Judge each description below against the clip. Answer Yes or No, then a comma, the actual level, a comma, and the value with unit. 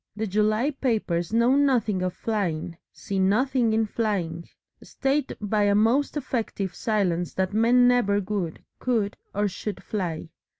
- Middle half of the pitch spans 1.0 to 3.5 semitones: No, average, 3.9 semitones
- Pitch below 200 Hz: No, high, 210 Hz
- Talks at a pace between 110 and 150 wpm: Yes, average, 140 wpm